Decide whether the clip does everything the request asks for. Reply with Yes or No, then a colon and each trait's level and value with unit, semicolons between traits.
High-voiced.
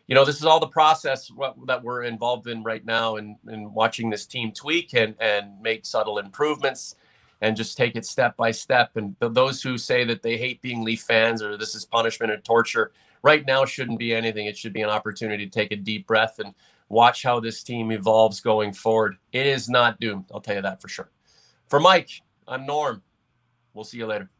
No: low, 115 Hz